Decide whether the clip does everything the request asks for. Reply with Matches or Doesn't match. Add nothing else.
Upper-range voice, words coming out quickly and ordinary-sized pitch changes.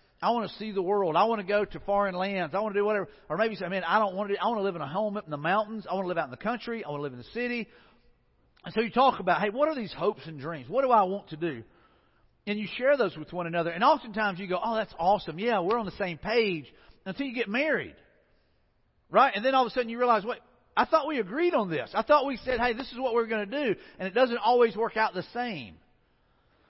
Matches